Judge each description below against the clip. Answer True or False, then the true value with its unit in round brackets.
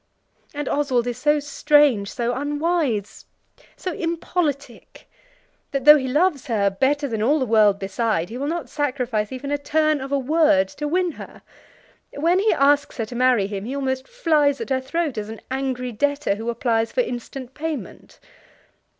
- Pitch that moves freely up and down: False (3.9 semitones)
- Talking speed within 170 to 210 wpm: True (175 wpm)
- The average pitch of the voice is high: True (275 Hz)